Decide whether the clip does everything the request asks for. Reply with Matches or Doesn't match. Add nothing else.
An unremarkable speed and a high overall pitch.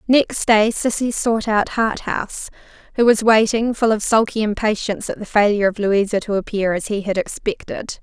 Matches